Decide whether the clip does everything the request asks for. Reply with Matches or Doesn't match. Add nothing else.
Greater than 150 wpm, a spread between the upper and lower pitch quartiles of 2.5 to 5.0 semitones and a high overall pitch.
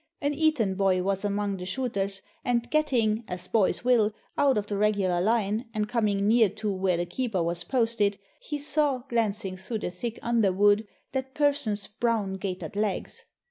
Matches